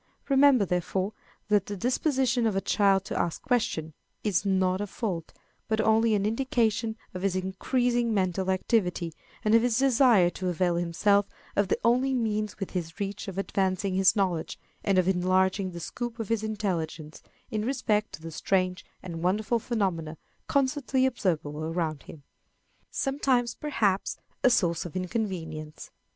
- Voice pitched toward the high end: Yes, high, 195 Hz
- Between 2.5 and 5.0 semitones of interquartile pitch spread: Yes, average, 4.1 semitones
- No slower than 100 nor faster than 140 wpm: No, average, 155 wpm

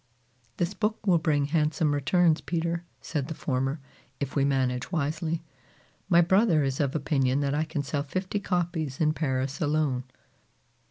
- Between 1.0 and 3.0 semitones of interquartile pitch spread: No, average, 3.4 semitones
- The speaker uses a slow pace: No, average, 155 wpm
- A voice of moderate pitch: Yes, medium, 155 Hz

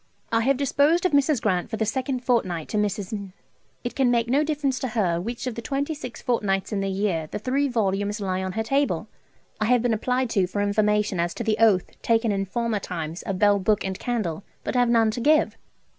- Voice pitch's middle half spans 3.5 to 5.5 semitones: Yes, average, 4.3 semitones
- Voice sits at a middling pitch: No, high, 220 Hz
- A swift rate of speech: Yes, fast, 225 wpm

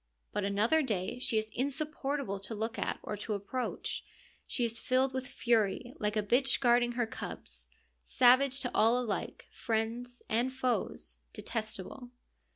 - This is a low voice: No, high, 240 Hz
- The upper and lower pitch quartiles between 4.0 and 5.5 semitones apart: No, average, 3.0 semitones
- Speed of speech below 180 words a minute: Yes, average, 150 wpm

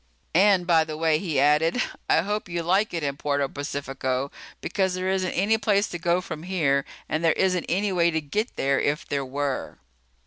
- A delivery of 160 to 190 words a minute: No, average, 200 wpm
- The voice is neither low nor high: Yes, medium, 165 Hz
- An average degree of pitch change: Yes, average, 4.5 semitones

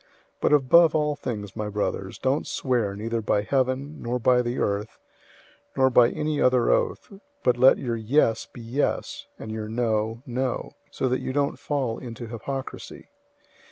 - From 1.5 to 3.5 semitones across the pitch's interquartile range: Yes, average, 3.0 semitones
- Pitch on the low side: Yes, low, 125 Hz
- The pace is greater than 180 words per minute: No, average, 165 wpm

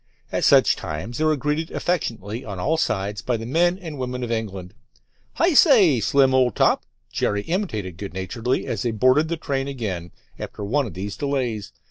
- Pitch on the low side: Yes, low, 125 Hz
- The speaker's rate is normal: Yes, average, 185 wpm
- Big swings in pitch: Yes, wide, 6.4 semitones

